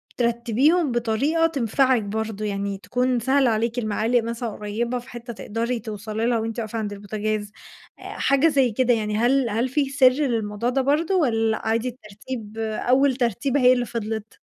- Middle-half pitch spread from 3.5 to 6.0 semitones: No, average, 2.9 semitones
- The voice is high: Yes, high, 235 Hz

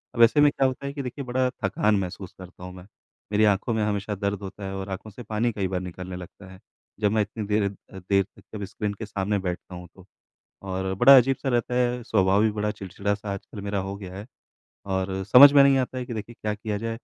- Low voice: Yes, low, 105 Hz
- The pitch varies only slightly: No, average, 3.5 semitones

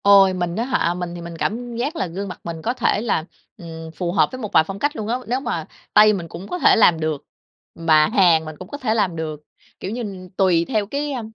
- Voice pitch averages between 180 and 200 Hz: Yes, high, 190 Hz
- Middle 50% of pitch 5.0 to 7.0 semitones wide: Yes, average, 5.3 semitones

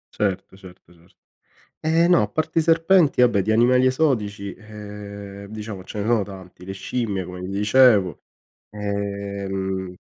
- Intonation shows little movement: No, average, 3.9 semitones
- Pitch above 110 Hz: No, low, 100 Hz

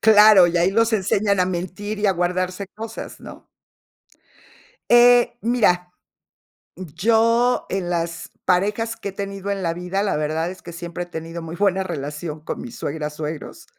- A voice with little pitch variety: No, average, 3.5 semitones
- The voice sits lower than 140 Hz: No, medium, 185 Hz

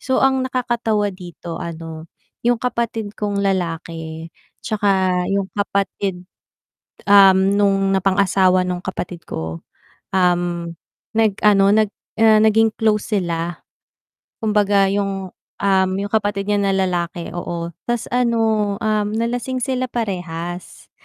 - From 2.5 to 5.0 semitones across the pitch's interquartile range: Yes, average, 3.4 semitones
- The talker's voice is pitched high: Yes, high, 195 Hz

